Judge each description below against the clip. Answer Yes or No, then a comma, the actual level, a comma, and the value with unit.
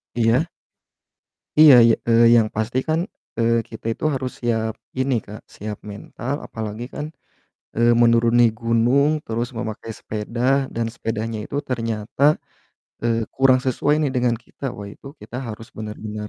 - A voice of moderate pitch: No, low, 115 Hz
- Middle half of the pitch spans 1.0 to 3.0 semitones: Yes, narrow, 2.4 semitones